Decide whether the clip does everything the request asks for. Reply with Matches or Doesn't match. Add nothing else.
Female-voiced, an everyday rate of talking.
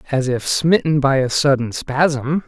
Doesn't match